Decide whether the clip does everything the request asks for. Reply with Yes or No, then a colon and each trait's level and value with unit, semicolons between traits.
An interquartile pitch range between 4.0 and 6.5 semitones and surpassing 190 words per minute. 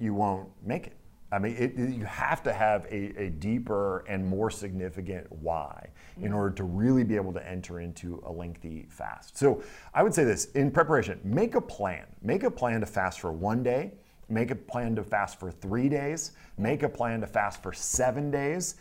Yes: average, 4.6 semitones; fast, 205 wpm